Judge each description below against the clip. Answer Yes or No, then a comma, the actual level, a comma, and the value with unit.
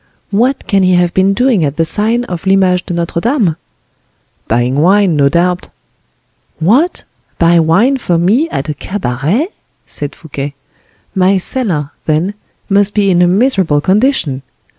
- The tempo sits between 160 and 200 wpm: No, average, 150 wpm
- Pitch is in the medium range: Yes, medium, 180 Hz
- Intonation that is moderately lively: Yes, average, 4.5 semitones